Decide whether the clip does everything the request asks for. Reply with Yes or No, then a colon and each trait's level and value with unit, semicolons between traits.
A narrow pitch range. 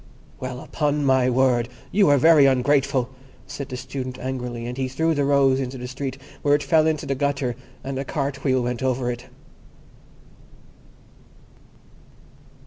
Yes: narrow, 2.0 semitones